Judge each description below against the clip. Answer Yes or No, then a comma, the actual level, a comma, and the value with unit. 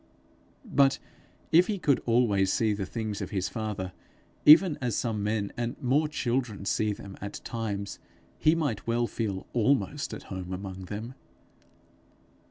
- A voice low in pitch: Yes, low, 110 Hz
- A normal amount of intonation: Yes, average, 4.5 semitones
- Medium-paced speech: Yes, average, 150 wpm